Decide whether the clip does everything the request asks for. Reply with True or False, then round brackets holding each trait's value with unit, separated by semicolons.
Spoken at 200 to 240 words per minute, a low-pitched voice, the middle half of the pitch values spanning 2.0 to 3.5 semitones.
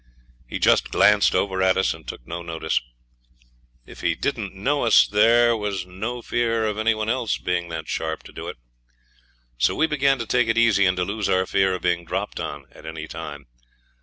False (205 wpm; 100 Hz; 4.7 semitones)